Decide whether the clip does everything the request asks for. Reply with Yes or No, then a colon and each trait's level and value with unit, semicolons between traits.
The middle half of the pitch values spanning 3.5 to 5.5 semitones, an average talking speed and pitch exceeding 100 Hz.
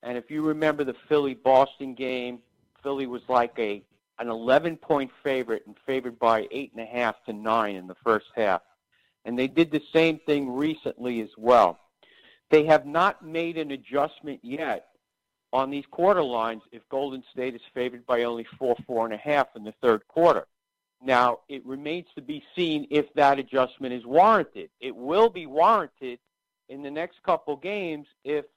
Yes: average, 4.1 semitones; average, 180 wpm; low, 135 Hz